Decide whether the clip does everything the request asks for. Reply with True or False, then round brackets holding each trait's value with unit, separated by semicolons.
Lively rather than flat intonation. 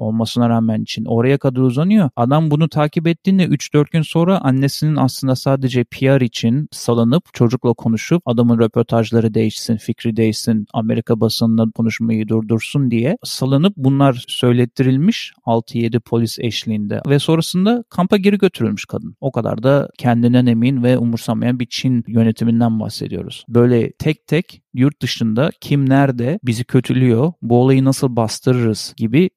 False (3.6 semitones)